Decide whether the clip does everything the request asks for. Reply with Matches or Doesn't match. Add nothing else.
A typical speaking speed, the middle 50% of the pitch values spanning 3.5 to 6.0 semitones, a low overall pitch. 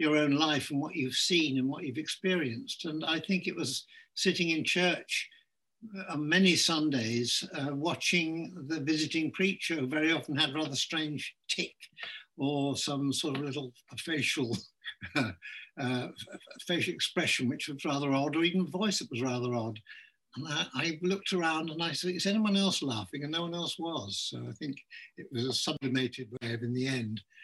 Doesn't match